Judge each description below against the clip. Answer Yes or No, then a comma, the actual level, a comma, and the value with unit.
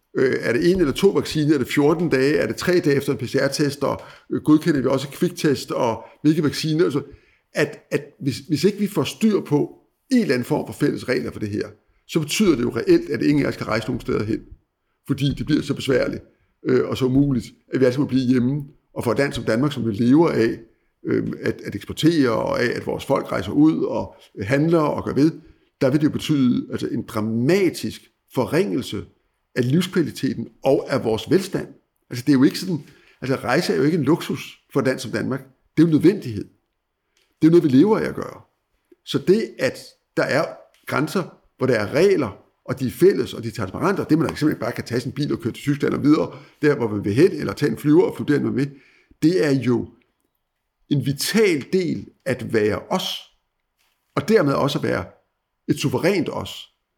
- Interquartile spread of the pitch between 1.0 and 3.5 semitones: No, average, 4.0 semitones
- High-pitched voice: No, medium, 145 Hz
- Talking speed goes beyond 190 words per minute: Yes, average, 220 wpm